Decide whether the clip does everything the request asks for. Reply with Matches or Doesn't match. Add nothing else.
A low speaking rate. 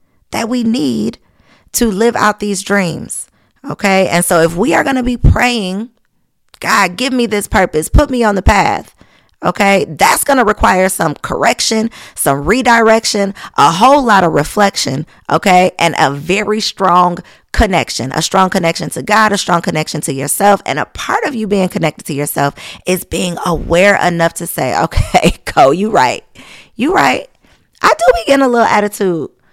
Doesn't match